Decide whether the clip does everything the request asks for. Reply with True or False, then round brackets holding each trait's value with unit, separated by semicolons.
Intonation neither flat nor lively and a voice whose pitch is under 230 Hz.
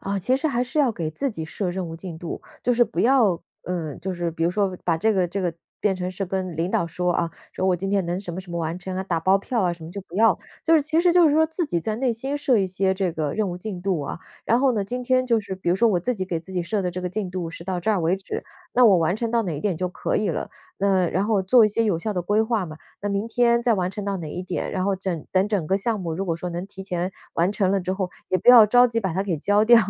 True (3.8 semitones; 190 Hz)